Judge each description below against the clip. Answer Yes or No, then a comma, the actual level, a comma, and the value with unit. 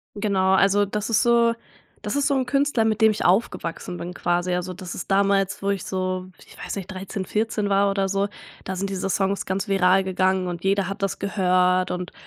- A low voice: No, high, 195 Hz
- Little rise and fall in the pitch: Yes, narrow, 1.7 semitones